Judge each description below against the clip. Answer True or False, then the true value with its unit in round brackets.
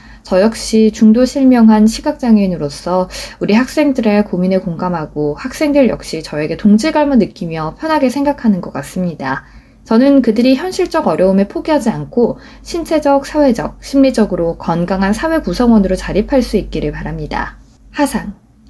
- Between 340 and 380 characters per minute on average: True (345 characters per minute)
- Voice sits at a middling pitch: False (215 Hz)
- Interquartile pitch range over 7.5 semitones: False (7.1 semitones)